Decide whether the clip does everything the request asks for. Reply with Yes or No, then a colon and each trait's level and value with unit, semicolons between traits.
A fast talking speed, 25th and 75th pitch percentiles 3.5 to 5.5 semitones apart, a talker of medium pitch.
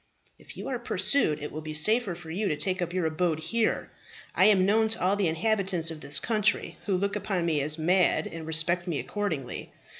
Yes: fast, 215 wpm; average, 4.3 semitones; medium, 175 Hz